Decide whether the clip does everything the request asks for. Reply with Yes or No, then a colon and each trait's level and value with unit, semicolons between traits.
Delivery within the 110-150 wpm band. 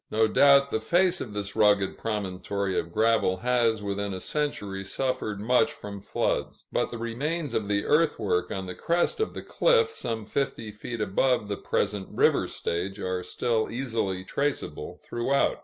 No: average, 165 wpm